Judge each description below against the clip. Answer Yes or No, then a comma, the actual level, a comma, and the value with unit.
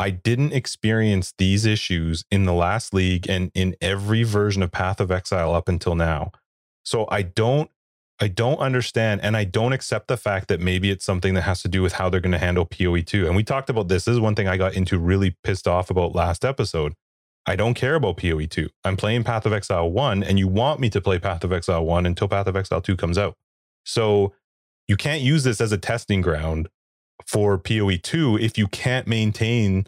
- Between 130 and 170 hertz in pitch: No, low, 100 Hz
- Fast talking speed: Yes, fast, 215 wpm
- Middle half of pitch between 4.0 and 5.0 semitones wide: No, average, 3.2 semitones